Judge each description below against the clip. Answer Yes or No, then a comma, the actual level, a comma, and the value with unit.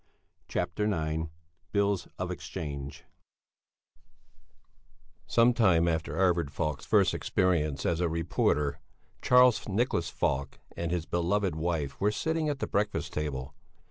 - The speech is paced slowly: Yes, slow, 120 wpm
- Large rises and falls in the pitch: No, average, 4.9 semitones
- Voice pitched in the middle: No, very low, 85 Hz